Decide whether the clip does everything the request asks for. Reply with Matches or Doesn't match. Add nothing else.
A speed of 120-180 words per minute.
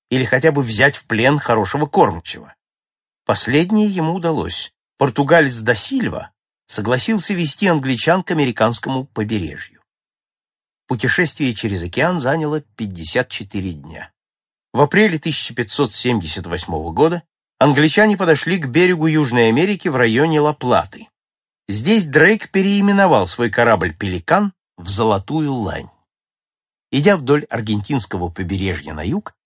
Doesn't match